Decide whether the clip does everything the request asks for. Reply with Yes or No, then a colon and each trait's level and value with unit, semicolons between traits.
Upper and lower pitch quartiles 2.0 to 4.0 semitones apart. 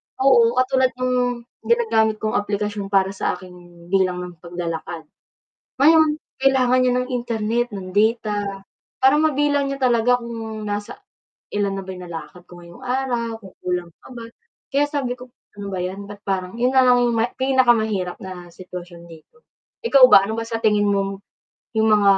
No: average, 4.8 semitones